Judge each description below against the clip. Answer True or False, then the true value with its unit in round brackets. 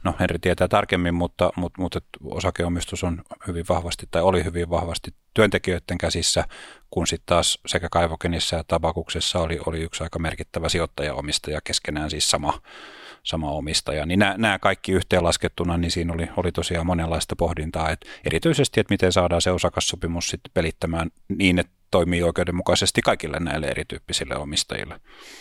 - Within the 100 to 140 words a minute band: False (150 wpm)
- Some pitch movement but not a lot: False (1.7 semitones)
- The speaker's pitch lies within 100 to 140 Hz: False (85 Hz)